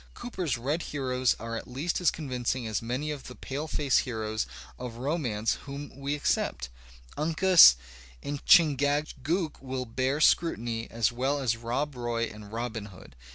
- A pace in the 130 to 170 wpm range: Yes, average, 150 wpm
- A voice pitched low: Yes, low, 130 Hz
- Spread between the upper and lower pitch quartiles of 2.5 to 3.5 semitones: No, average, 4.1 semitones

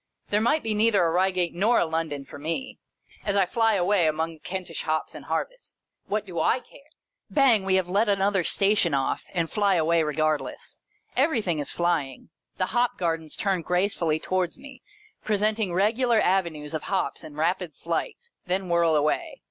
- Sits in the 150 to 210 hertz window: Yes, medium, 185 Hz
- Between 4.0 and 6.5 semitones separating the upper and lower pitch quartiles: Yes, average, 4.4 semitones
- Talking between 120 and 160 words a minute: No, average, 170 wpm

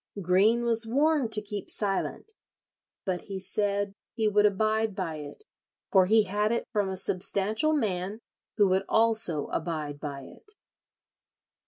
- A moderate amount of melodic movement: Yes, average, 3.0 semitones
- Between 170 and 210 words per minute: No, average, 145 wpm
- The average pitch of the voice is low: No, high, 205 Hz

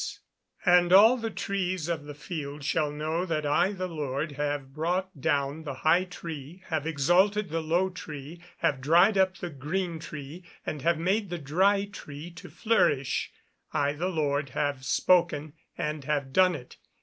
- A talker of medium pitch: Yes, medium, 160 Hz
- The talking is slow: No, average, 170 wpm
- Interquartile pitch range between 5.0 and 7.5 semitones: No, average, 4.0 semitones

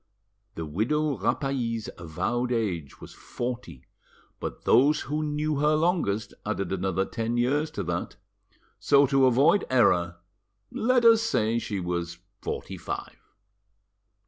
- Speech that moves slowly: Yes, slow, 125 wpm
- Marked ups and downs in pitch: Yes, wide, 7.3 semitones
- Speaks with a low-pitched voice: Yes, low, 120 Hz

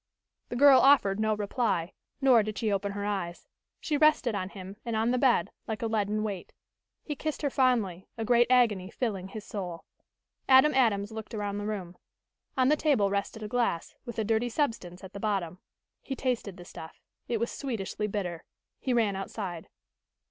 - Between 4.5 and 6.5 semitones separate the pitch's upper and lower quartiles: No, average, 3.8 semitones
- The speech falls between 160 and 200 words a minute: Yes, average, 185 wpm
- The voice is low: No, high, 215 Hz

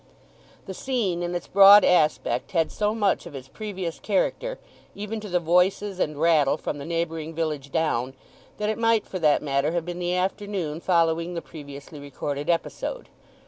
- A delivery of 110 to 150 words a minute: No, average, 175 wpm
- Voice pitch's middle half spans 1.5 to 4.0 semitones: No, average, 4.4 semitones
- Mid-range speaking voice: Yes, medium, 170 Hz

